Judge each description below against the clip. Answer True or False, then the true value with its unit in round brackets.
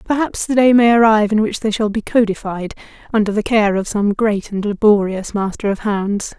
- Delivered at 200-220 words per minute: True (205 wpm)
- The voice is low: False (210 Hz)